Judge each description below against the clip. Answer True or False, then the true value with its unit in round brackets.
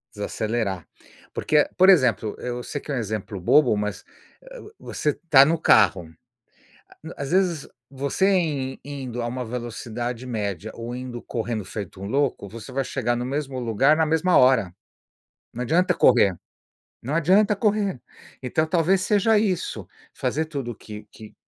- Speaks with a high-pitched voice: False (130 Hz)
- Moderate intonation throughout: False (5.9 semitones)